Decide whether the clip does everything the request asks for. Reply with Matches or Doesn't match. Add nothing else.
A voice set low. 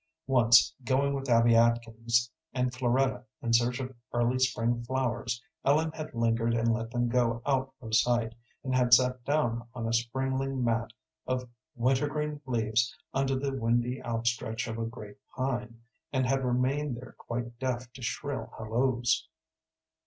Matches